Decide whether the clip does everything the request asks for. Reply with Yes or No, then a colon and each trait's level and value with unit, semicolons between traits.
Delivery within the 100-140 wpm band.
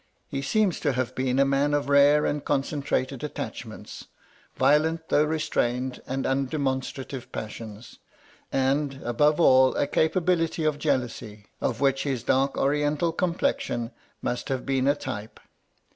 Yes: slow, 135 wpm